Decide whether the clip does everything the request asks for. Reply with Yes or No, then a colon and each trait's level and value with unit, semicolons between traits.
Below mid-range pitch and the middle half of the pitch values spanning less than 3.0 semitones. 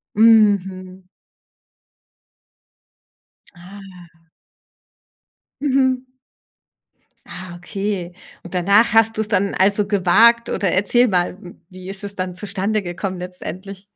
No: high, 195 Hz; narrow, 2.6 semitones